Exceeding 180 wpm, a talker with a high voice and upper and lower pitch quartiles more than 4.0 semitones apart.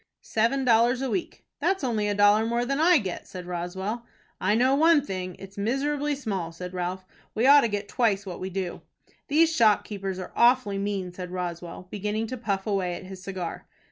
Yes: average, 200 wpm; high, 205 Hz; average, 4.9 semitones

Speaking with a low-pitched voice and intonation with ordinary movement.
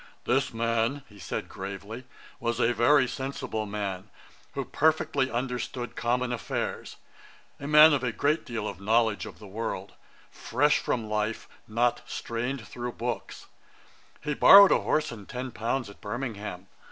Yes: low, 120 Hz; average, 3.6 semitones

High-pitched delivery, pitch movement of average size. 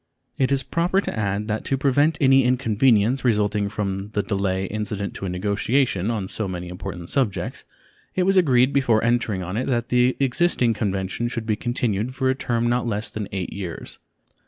No: low, 115 Hz; average, 4.4 semitones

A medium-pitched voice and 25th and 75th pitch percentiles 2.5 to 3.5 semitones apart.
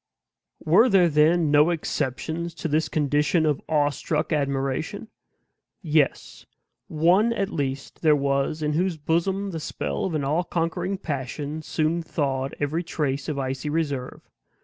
Yes: medium, 155 Hz; average, 2.9 semitones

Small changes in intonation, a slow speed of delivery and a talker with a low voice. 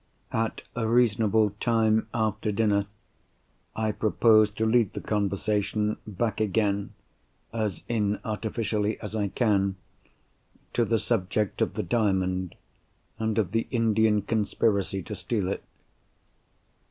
Yes: narrow, 1.8 semitones; slow, 110 wpm; low, 105 Hz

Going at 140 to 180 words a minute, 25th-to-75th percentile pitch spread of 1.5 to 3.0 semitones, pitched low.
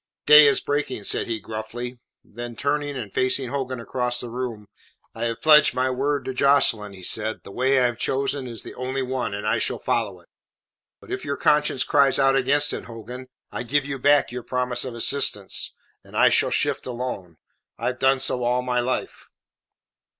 No: average, 195 wpm; narrow, 2.6 semitones; low, 125 Hz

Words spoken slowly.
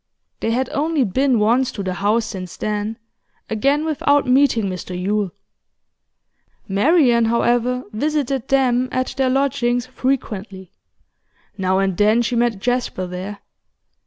Yes: slow, 130 wpm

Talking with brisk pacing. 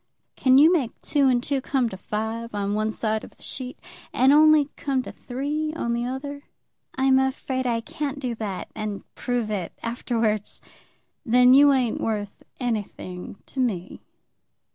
No: average, 165 wpm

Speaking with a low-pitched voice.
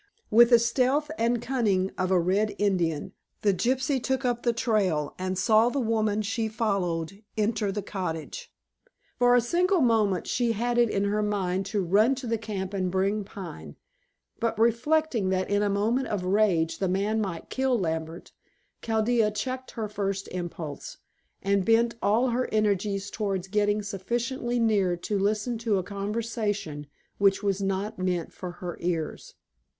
No: high, 210 Hz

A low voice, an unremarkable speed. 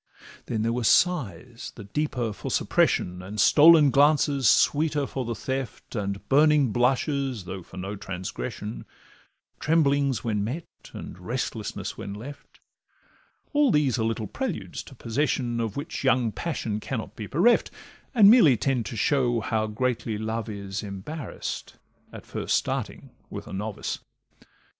Yes: low, 120 Hz; average, 145 wpm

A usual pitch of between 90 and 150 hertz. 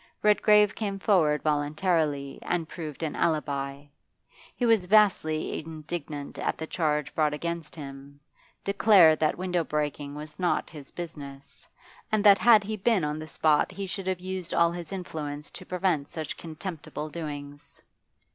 No: medium, 160 Hz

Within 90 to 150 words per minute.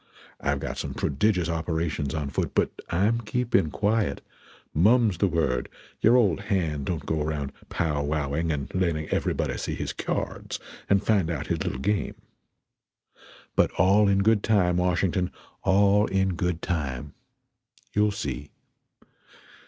Yes: average, 140 wpm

